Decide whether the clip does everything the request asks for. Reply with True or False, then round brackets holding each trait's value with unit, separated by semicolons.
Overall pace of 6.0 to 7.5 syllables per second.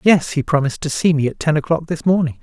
True (6.6 syllables/s)